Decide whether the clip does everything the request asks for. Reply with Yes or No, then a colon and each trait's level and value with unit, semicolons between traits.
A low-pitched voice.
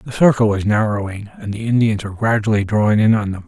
Yes: low, 110 Hz